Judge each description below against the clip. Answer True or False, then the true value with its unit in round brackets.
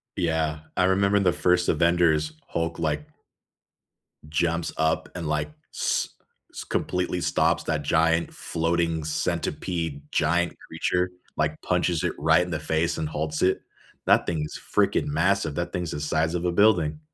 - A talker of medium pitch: False (85 Hz)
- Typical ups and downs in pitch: False (2.2 semitones)